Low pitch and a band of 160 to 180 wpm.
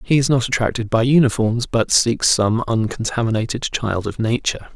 Yes: low, 115 Hz; average, 165 wpm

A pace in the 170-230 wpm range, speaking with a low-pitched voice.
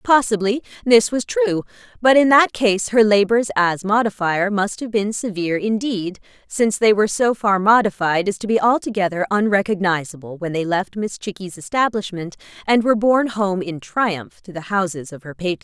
No: average, 175 wpm; high, 205 Hz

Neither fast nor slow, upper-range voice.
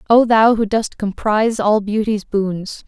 Yes: average, 165 wpm; high, 210 Hz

